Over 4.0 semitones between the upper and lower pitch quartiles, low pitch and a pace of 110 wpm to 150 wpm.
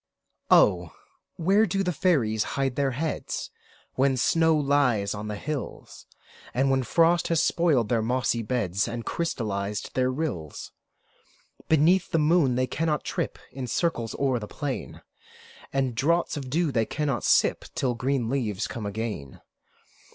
Yes: wide, 5.5 semitones; low, 130 Hz; average, 140 wpm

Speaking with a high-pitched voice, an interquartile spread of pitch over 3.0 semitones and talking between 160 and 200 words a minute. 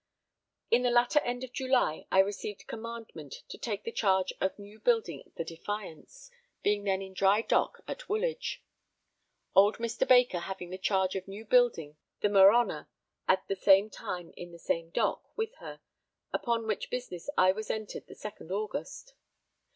Yes: high, 205 Hz; average, 3.9 semitones; average, 165 wpm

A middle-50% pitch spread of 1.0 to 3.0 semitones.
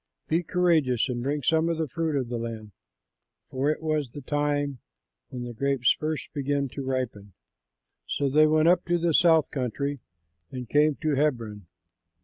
No: average, 3.6 semitones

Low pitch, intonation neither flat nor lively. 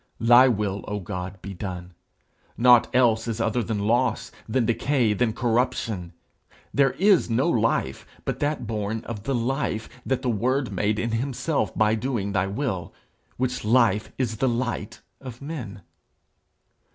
Yes: low, 115 Hz; average, 3.4 semitones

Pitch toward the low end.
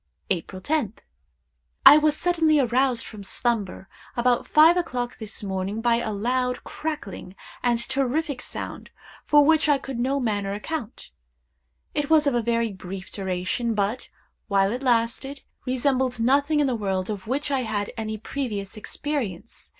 No: high, 240 Hz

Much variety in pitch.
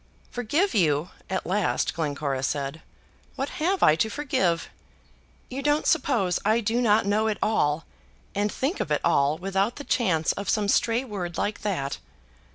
Yes: wide, 6.5 semitones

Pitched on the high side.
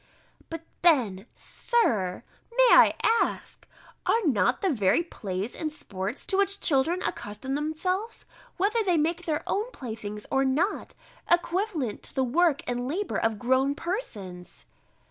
Yes: very high, 295 Hz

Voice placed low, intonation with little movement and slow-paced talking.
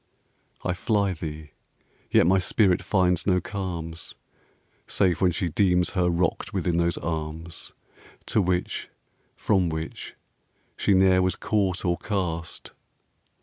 Yes: very low, 90 Hz; narrow, 2.2 semitones; slow, 125 wpm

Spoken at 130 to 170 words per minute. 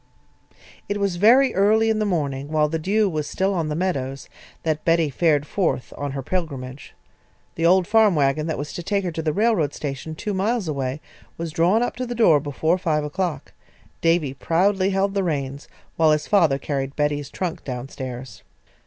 No: average, 190 wpm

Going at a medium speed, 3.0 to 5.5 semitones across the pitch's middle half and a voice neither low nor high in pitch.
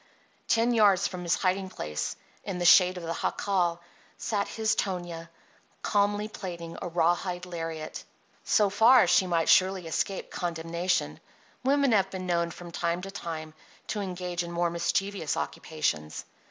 No: average, 150 wpm; narrow, 2.6 semitones; medium, 180 Hz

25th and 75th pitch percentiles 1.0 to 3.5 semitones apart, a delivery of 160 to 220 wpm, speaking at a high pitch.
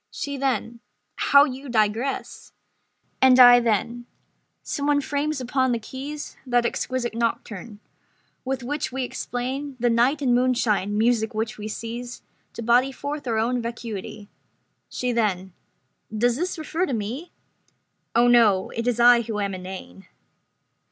No: average, 2.9 semitones; average, 145 wpm; high, 240 Hz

